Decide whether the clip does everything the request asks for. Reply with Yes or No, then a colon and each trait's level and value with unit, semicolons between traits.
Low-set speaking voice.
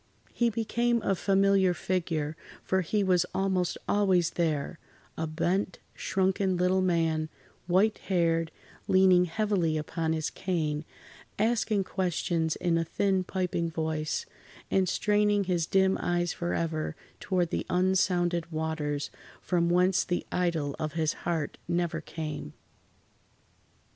No: medium, 175 Hz